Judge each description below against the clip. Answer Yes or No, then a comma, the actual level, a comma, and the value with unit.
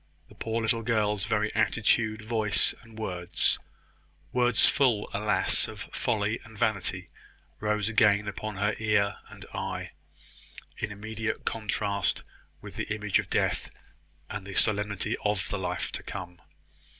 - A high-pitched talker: No, low, 105 Hz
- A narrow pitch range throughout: Yes, narrow, 1.6 semitones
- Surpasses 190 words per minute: No, average, 140 wpm